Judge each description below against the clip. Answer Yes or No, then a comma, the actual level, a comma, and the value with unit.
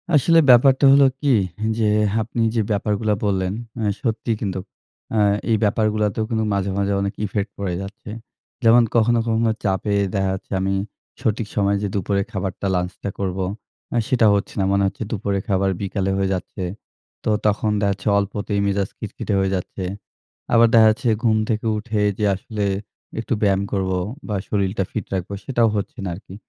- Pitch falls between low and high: No, low, 105 Hz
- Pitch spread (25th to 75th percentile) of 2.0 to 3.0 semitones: Yes, narrow, 2.4 semitones